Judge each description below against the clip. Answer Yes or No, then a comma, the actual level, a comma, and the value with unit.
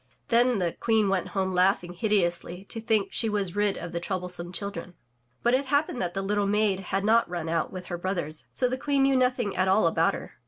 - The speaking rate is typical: No, fast, 225 wpm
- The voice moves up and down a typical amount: Yes, average, 3.9 semitones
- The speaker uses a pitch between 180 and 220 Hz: Yes, high, 195 Hz